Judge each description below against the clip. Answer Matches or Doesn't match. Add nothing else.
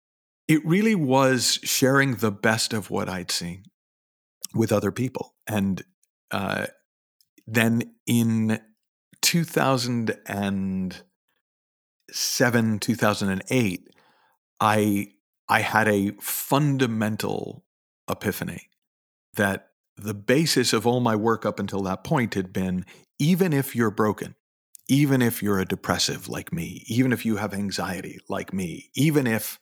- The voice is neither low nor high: Doesn't match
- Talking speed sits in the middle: Doesn't match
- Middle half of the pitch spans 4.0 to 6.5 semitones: Matches